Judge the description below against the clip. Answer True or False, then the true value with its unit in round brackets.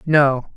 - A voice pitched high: False (140 Hz)